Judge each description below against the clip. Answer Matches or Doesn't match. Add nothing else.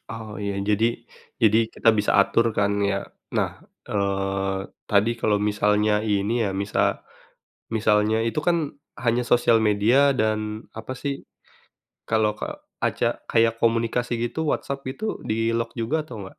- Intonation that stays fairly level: Matches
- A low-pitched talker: Matches